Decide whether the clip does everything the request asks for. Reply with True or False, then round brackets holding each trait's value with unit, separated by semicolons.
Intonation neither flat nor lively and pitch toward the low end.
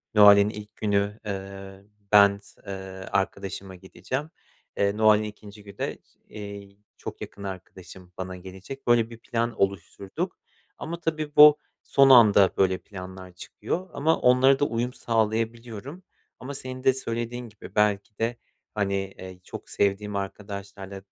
True (3.3 semitones; 105 Hz)